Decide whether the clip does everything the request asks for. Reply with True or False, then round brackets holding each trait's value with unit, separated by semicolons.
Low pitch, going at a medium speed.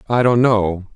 True (110 Hz; 190 wpm)